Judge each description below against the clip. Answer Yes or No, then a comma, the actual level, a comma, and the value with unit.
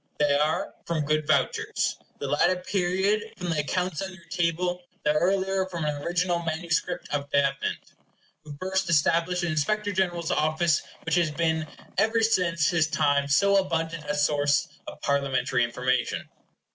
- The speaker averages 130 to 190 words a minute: Yes, average, 155 wpm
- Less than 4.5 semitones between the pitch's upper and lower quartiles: Yes, average, 3.4 semitones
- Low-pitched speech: No, medium, 165 Hz